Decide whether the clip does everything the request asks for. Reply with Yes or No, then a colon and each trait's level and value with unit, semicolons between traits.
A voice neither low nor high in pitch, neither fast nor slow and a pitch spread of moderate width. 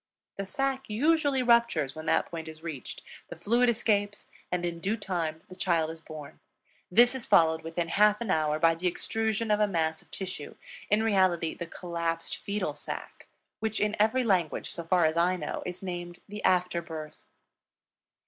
Yes: medium, 180 Hz; average, 180 wpm; average, 4.3 semitones